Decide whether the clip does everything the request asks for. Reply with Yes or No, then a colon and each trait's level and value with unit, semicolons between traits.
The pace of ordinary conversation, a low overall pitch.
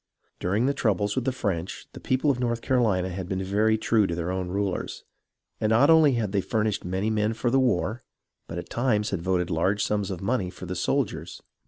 No: fast, 215 wpm; low, 105 Hz